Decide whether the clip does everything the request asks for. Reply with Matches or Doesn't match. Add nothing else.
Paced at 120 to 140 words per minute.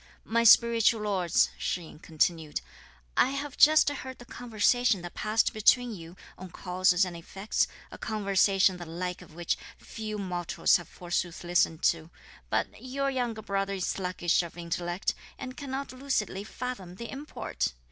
Doesn't match